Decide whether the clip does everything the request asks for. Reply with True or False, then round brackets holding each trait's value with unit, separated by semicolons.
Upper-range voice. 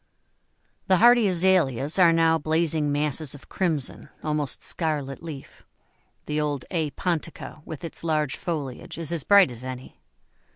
False (155 Hz)